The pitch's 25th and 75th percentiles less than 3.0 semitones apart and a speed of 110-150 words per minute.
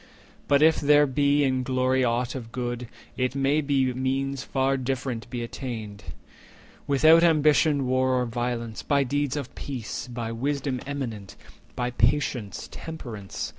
Yes: narrow, 2.6 semitones; average, 145 wpm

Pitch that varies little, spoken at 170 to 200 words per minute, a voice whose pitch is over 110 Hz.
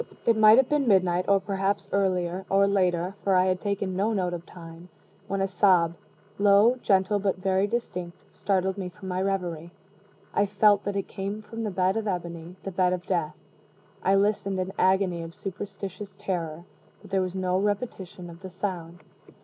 Yes: narrow, 1.9 semitones; average, 190 wpm; high, 190 Hz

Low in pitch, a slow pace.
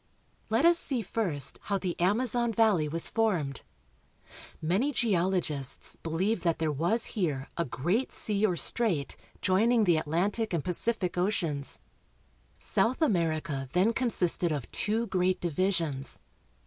No: medium, 185 Hz; slow, 130 wpm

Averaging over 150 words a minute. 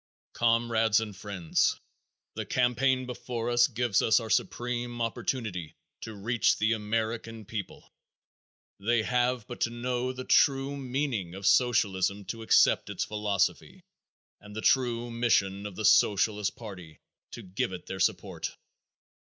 No: average, 140 wpm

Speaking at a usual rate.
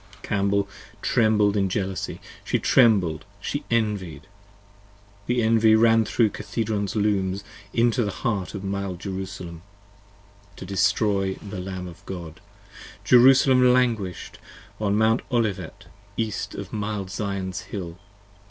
No: slow, 115 wpm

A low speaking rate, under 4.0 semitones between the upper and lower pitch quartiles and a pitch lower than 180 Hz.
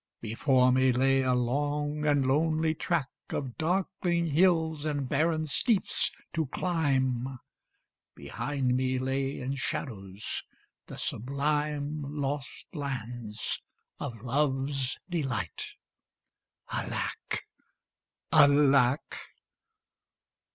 Yes: slow, 90 wpm; average, 2.8 semitones; medium, 140 Hz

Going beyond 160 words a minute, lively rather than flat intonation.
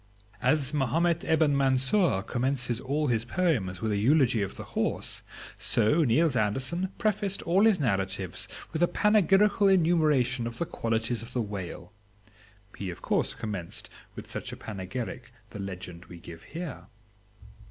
No: average, 150 wpm; wide, 7.8 semitones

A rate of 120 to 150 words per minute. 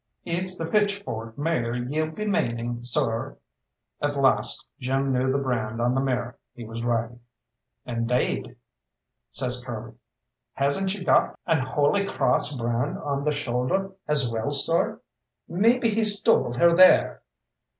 Yes: average, 140 wpm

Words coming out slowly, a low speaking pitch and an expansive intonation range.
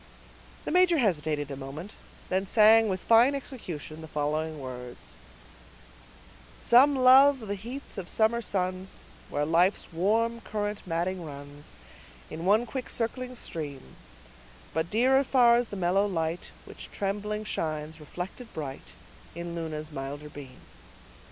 No: slow, 130 wpm; medium, 185 Hz; wide, 6.7 semitones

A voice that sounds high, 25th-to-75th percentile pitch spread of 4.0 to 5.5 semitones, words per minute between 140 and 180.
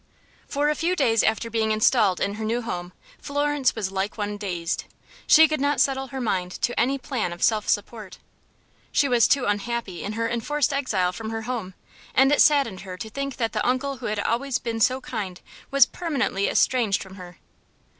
No: high, 230 Hz; average, 4.9 semitones; average, 195 wpm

